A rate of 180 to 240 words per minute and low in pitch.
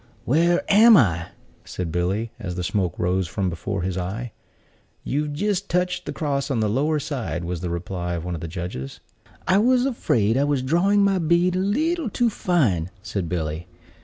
Yes: average, 190 wpm; low, 120 Hz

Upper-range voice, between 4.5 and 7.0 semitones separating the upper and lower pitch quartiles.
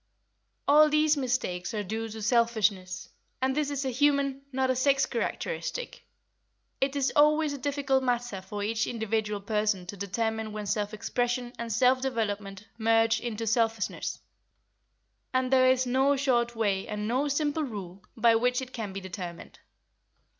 No: high, 235 Hz; average, 4.0 semitones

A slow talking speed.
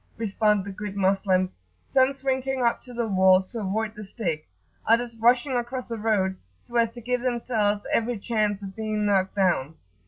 No: average, 180 wpm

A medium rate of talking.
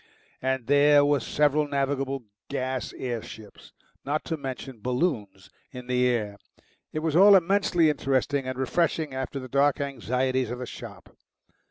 Yes: average, 150 wpm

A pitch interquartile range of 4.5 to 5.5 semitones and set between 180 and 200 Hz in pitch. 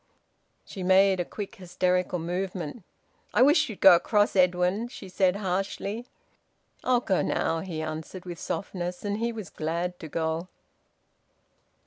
No: narrow, 2.6 semitones; medium, 185 Hz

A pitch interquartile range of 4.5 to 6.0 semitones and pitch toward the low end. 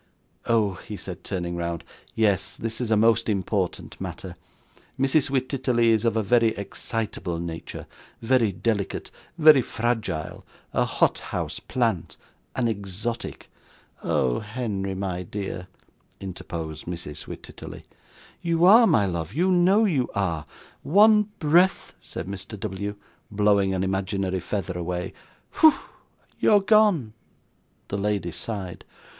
Yes: average, 5.0 semitones; low, 105 Hz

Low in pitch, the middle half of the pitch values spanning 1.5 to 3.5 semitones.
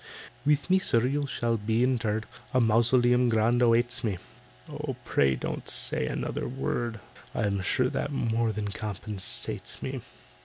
Yes: low, 115 Hz; narrow, 2.6 semitones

